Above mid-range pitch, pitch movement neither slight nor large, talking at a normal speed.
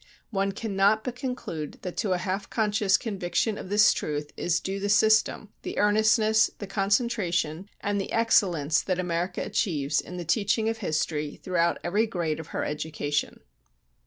Yes: high, 195 Hz; average, 4.0 semitones; average, 160 wpm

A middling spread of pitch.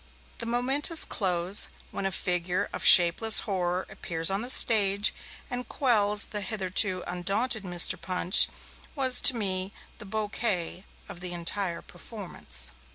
Yes: average, 3.7 semitones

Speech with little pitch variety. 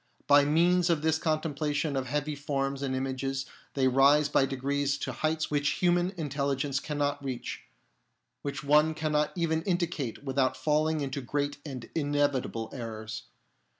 Yes: narrow, 2.3 semitones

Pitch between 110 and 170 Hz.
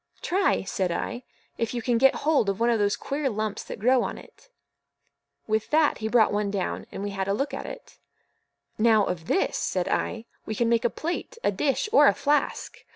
No: high, 230 Hz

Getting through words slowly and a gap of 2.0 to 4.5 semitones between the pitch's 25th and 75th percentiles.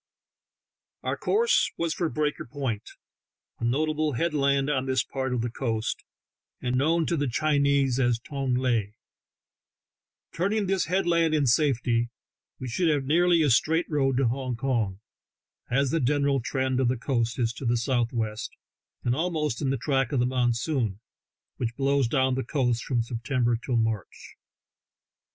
No: average, 160 wpm; average, 3.8 semitones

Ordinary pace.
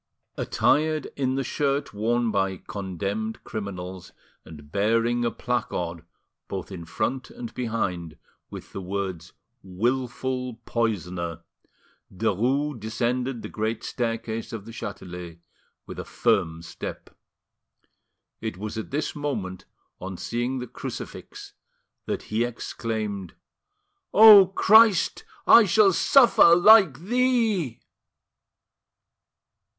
No: slow, 105 wpm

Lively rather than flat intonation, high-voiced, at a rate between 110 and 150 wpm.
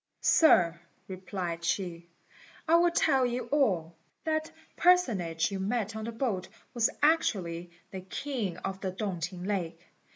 Yes: wide, 6.3 semitones; high, 195 Hz; average, 140 wpm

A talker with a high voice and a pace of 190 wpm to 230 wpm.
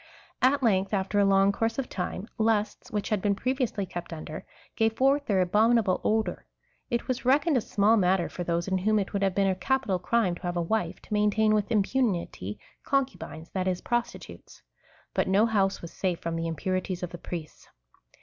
Yes: high, 200 Hz; average, 195 wpm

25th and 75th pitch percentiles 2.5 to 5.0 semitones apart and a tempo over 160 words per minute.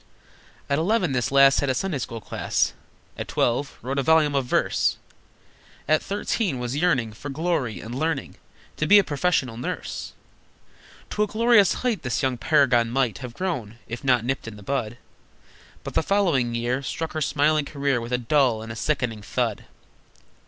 Yes: average, 4.7 semitones; average, 175 wpm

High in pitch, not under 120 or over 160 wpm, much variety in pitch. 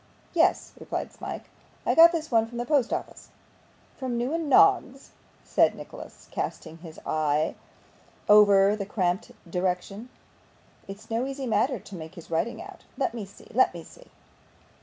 Yes: high, 225 Hz; average, 155 wpm; wide, 6.3 semitones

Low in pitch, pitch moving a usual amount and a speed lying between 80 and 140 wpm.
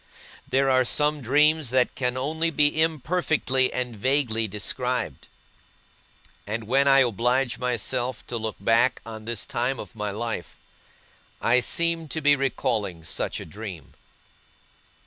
Yes: low, 125 Hz; average, 3.6 semitones; slow, 135 wpm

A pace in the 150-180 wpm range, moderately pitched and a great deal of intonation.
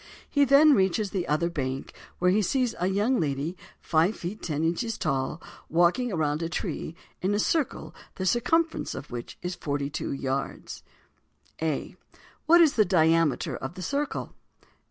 Yes: average, 160 wpm; medium, 175 Hz; wide, 6.5 semitones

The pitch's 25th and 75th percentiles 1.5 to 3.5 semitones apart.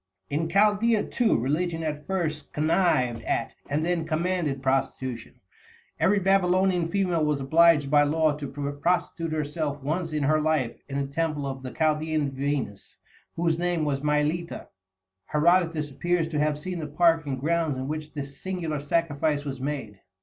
Yes: average, 2.9 semitones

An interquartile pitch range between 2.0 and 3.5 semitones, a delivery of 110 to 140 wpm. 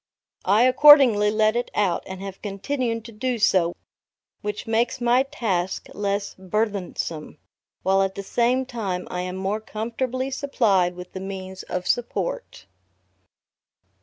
No: average, 4.2 semitones; slow, 135 wpm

